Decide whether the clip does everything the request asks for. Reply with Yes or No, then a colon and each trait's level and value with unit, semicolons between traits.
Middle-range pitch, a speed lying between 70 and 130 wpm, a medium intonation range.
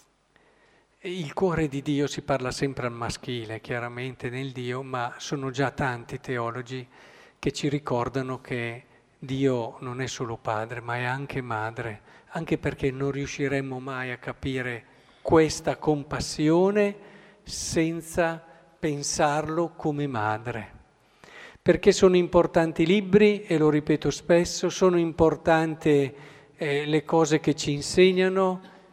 Yes: medium, 145 Hz; average, 125 wpm; average, 4.5 semitones